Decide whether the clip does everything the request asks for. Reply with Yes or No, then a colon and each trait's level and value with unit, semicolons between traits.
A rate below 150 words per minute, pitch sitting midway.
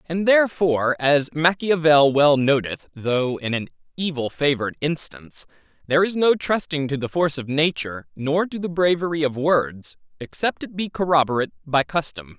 No: average, 160 wpm; medium, 150 Hz